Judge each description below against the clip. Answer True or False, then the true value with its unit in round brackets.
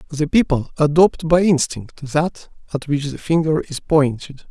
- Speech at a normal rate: True (160 wpm)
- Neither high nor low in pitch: True (150 Hz)